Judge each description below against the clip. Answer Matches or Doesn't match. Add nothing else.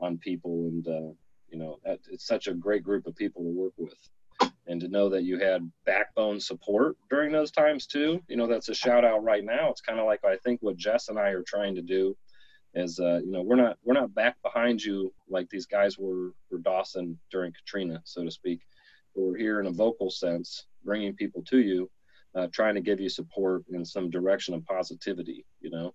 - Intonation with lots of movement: Doesn't match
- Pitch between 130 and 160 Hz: Doesn't match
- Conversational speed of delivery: Doesn't match